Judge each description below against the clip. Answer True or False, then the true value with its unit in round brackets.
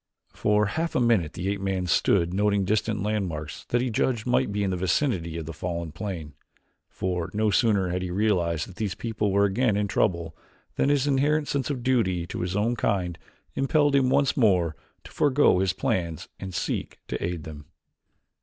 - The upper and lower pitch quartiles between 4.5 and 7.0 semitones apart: True (5.1 semitones)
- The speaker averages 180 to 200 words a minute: True (190 wpm)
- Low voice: True (100 Hz)